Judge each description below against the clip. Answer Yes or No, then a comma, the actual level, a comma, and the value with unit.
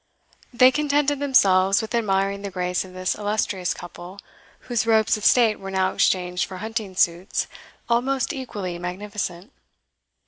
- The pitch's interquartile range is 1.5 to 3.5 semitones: No, average, 4.2 semitones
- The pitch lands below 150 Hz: No, high, 200 Hz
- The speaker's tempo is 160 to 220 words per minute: No, average, 140 wpm